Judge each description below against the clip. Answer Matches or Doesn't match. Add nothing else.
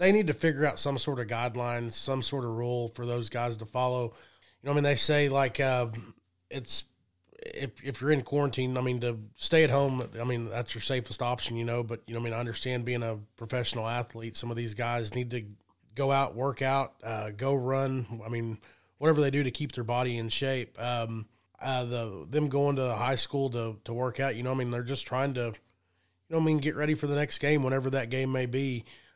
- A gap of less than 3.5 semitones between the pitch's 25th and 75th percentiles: Matches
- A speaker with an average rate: Doesn't match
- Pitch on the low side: Matches